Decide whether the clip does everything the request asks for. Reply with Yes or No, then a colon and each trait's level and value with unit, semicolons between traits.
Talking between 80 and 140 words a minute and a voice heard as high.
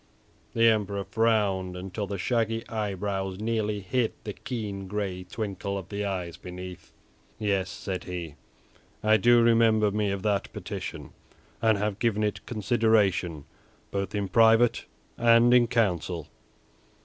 No: slow, 135 wpm; low, 105 Hz